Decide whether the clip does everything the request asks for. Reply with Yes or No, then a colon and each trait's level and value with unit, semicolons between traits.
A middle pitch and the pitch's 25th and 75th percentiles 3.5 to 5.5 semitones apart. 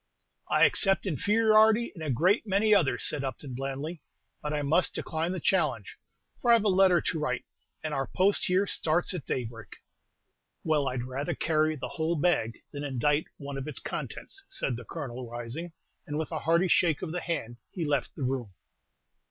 Yes: medium, 155 Hz; average, 5.0 semitones